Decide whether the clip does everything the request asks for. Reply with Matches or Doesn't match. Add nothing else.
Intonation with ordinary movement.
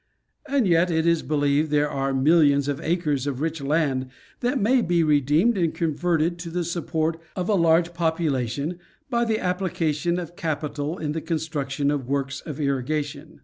Matches